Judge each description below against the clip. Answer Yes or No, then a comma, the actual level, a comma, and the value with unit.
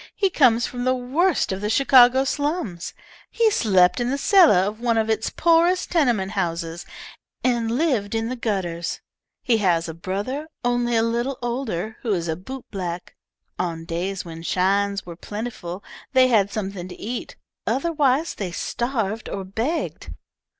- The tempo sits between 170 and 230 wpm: No, average, 155 wpm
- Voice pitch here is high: Yes, high, 225 Hz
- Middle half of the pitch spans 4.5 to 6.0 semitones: Yes, wide, 5.4 semitones